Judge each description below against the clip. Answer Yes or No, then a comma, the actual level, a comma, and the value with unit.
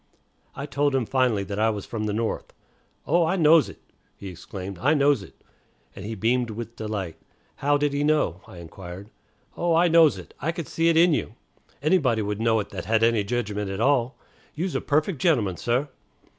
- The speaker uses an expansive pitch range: Yes, wide, 6.2 semitones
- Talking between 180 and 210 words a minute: Yes, average, 200 wpm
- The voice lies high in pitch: No, low, 120 Hz